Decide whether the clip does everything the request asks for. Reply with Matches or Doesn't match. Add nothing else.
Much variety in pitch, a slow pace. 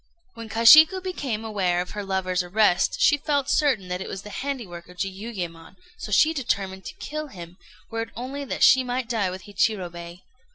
Doesn't match